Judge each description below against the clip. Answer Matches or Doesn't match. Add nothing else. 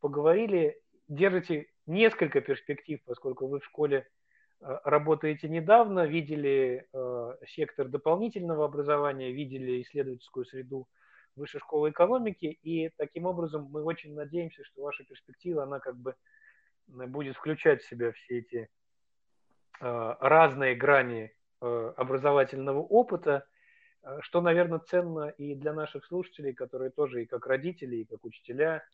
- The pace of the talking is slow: Doesn't match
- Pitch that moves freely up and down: Doesn't match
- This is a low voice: Doesn't match